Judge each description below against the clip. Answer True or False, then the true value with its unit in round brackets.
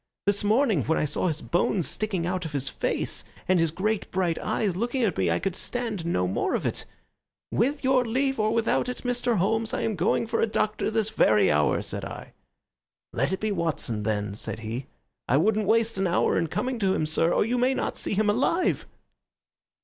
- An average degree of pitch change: False (5.8 semitones)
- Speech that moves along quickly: True (210 wpm)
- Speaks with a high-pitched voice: True (200 Hz)